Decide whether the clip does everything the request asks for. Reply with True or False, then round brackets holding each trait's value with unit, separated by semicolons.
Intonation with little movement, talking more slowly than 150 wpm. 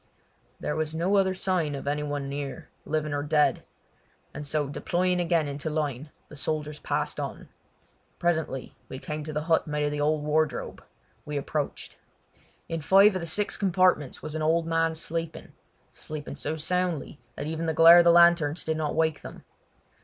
False (2.3 semitones; 175 wpm)